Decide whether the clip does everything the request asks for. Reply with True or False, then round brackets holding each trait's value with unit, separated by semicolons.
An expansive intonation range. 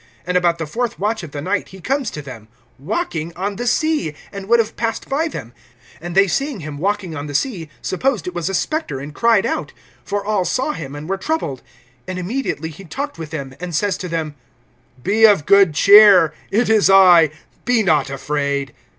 True (6.2 semitones)